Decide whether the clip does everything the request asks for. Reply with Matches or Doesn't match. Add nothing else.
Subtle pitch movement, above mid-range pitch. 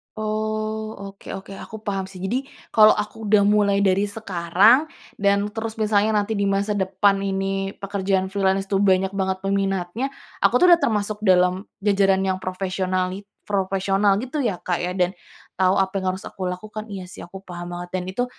Matches